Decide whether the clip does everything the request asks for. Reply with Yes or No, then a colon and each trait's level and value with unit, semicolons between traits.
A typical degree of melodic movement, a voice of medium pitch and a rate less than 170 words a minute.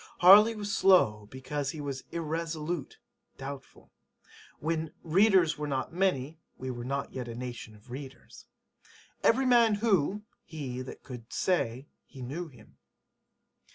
No: wide, 5.8 semitones; medium, 150 Hz; slow, 135 wpm